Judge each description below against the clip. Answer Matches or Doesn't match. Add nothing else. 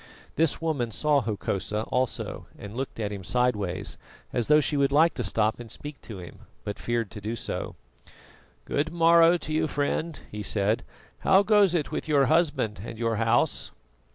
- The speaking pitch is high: Doesn't match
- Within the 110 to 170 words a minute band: Doesn't match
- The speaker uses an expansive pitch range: Matches